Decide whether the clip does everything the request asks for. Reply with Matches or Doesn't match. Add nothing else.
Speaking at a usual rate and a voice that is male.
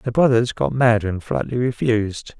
Matches